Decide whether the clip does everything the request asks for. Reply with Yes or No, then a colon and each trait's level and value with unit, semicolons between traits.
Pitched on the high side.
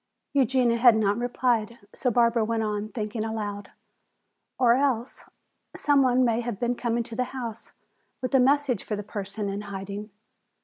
Yes: high, 230 Hz